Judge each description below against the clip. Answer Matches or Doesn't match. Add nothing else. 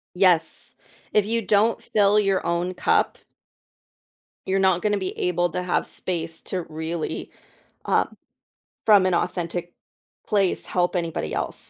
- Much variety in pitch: Doesn't match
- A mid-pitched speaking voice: Matches